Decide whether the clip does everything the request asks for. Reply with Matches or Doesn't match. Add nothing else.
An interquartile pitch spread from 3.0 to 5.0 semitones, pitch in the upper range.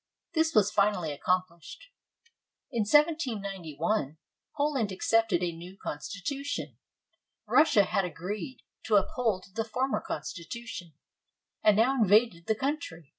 Doesn't match